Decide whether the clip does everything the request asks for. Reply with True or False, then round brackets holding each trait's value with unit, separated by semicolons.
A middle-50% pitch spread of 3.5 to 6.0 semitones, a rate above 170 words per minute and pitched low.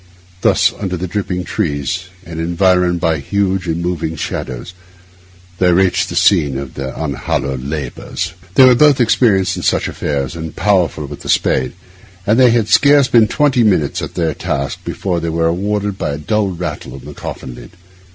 True (5.1 semitones; 180 wpm; 90 Hz)